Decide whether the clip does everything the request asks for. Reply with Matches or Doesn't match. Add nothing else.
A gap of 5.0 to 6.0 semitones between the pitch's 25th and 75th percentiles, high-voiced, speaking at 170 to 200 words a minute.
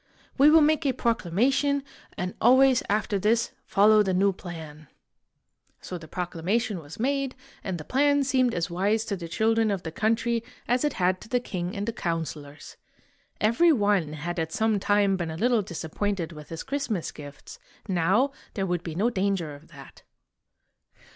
Matches